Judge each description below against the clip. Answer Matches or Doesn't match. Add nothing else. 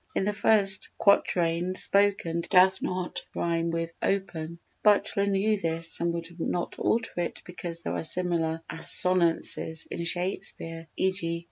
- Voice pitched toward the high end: Doesn't match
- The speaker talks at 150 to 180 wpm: Doesn't match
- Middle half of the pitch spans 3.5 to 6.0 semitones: Doesn't match